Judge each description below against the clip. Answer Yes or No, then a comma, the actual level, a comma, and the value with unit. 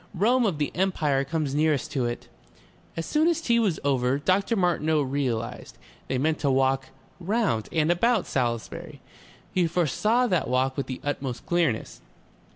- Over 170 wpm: No, average, 160 wpm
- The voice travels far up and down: Yes, wide, 5.8 semitones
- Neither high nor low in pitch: Yes, medium, 150 Hz